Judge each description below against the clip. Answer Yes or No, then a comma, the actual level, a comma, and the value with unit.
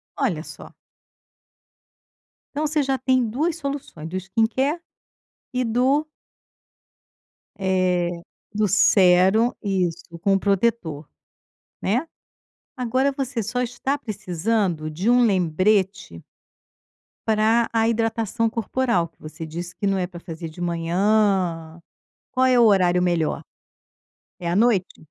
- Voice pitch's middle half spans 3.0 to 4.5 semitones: No, average, 5.3 semitones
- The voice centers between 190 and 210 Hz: Yes, high, 205 Hz